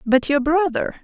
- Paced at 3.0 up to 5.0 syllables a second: Yes, 4.6 syllables/s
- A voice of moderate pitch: No, very high, 295 Hz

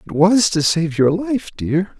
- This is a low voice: No, medium, 180 Hz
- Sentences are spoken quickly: Yes, fast, 210 wpm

